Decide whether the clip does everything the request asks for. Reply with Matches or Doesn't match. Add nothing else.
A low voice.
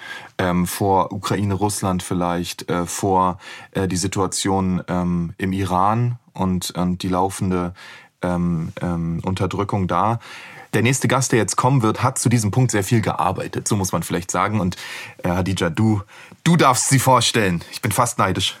Matches